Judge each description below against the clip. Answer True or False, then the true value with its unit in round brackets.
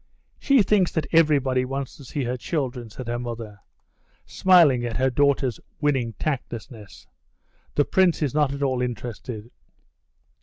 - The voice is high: False (130 Hz)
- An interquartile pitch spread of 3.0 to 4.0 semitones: True (3.5 semitones)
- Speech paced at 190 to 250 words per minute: False (145 wpm)